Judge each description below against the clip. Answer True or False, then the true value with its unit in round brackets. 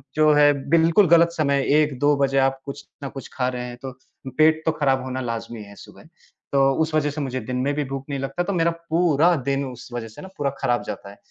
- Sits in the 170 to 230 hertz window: False (140 Hz)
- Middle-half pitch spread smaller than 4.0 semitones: True (3.0 semitones)